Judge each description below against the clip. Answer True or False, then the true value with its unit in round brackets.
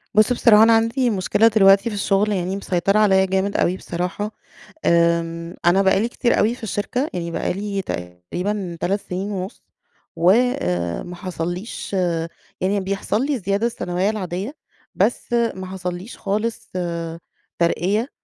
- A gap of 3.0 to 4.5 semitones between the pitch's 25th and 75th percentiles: True (3.3 semitones)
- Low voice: False (195 Hz)